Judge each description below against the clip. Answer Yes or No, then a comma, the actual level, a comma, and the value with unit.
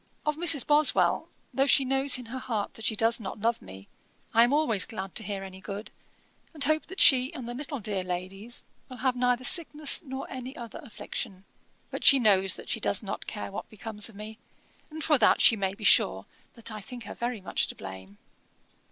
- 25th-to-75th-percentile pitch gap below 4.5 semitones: No, average, 5.0 semitones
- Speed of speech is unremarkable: No, fast, 210 wpm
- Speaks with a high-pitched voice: Yes, high, 230 Hz